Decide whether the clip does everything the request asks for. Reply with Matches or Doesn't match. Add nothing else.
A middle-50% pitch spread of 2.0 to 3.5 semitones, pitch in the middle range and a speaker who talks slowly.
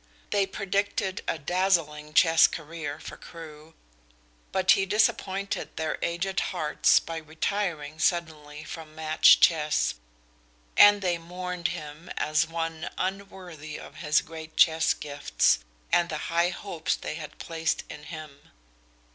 Matches